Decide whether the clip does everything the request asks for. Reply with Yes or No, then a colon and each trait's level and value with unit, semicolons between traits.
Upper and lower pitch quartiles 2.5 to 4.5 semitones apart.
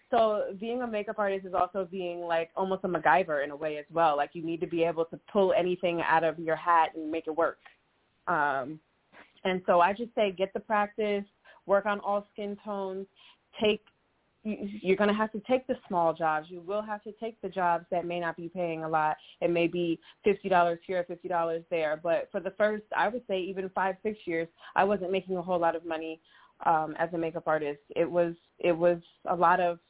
Yes: average, 3.5 semitones